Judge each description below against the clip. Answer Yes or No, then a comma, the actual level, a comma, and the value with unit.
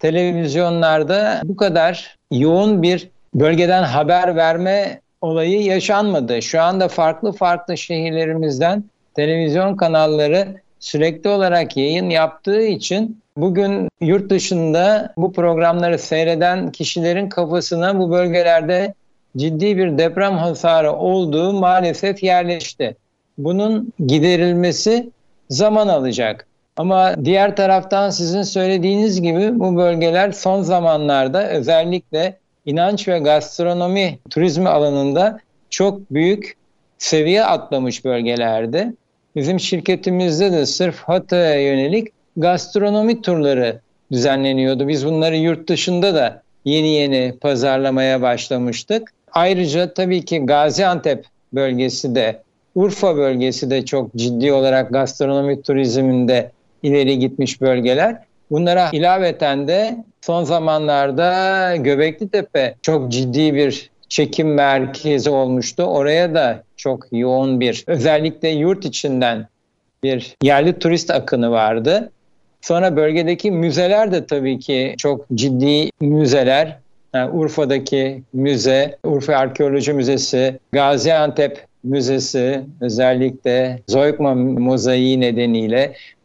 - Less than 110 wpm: Yes, average, 100 wpm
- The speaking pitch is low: No, medium, 160 Hz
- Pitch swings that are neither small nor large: Yes, average, 4.9 semitones